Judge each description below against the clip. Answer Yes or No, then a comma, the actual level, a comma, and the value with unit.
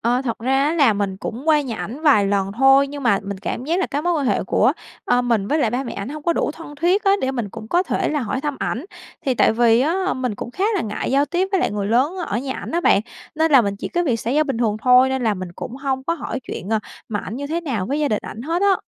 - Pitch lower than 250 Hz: No, very high, 265 Hz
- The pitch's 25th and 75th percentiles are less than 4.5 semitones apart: No, average, 5.2 semitones